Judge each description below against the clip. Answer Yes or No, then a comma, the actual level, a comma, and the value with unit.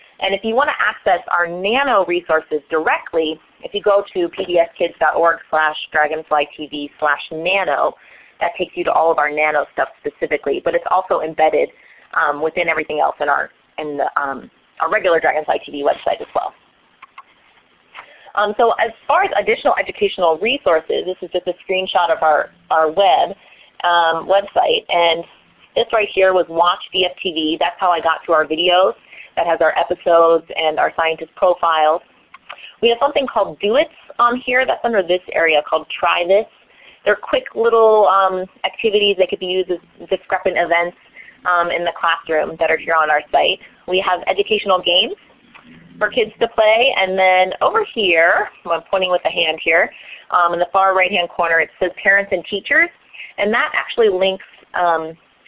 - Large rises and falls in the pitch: No, average, 3.5 semitones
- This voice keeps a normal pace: Yes, average, 175 wpm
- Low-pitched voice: No, medium, 180 Hz